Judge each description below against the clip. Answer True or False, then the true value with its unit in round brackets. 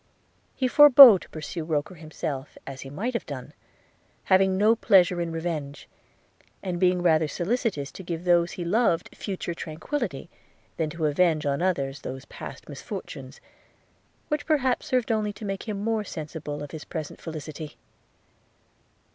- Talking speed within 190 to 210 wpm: False (155 wpm)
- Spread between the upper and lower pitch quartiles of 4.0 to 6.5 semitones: True (5.1 semitones)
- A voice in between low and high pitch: True (175 Hz)